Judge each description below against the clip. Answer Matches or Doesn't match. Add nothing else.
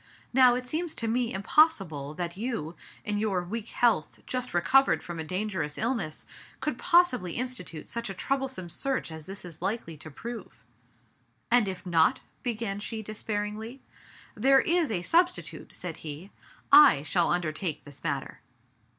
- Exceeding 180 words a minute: Doesn't match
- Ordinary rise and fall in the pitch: Doesn't match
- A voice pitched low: Doesn't match